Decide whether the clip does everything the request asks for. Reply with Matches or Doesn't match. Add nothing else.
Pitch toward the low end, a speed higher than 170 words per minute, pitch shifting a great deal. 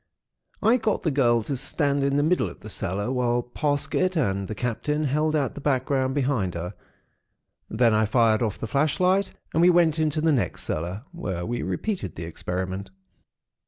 Matches